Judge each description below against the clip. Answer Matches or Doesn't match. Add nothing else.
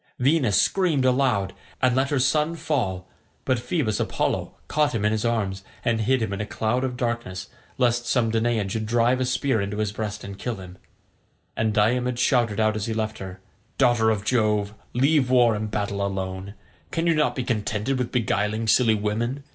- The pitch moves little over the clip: Doesn't match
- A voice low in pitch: Matches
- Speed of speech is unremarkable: Matches